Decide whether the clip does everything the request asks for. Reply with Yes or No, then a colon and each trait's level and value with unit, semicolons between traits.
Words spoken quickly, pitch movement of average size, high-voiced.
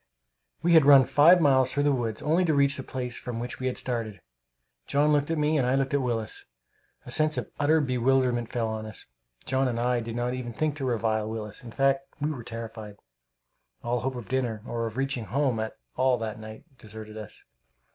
No: fast, 215 wpm; average, 3.4 semitones; low, 125 Hz